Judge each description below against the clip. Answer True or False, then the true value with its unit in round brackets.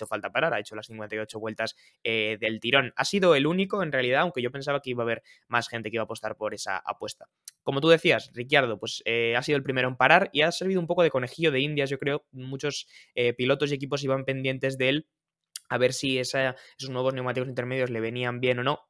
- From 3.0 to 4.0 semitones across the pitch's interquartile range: True (3.4 semitones)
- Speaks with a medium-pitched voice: False (130 Hz)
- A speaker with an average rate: False (245 wpm)